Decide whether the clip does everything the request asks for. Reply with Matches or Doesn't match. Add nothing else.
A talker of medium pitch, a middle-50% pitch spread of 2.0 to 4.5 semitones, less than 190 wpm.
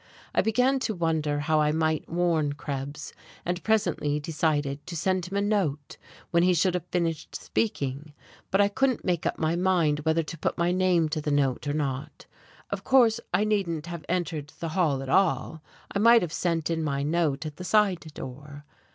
Doesn't match